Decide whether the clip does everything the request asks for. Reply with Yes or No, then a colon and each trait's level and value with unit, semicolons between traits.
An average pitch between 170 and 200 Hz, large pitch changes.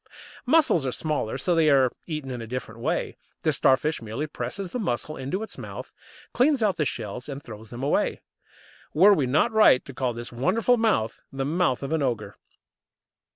No: medium, 140 Hz; wide, 6.4 semitones